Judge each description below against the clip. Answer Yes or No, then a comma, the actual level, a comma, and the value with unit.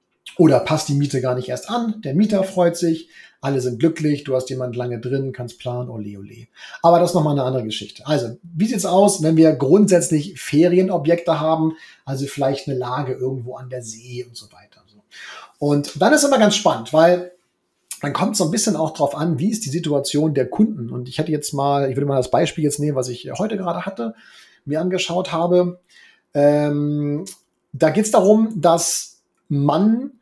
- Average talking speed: No, fast, 205 wpm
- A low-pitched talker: No, medium, 150 Hz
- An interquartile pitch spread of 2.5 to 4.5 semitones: No, average, 5.2 semitones